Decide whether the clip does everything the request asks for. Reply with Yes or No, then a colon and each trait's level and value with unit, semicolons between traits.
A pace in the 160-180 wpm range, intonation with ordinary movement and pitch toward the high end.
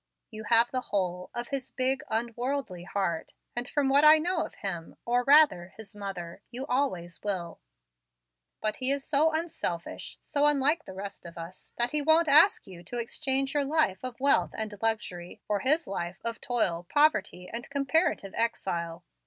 No: average, 175 wpm; wide, 6.8 semitones; high, 235 Hz